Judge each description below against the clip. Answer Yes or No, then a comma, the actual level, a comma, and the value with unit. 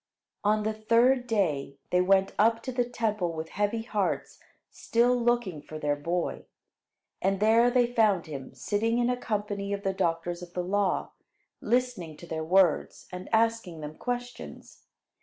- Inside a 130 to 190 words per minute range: Yes, average, 160 wpm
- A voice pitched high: Yes, high, 205 Hz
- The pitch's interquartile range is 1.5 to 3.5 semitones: No, average, 4.8 semitones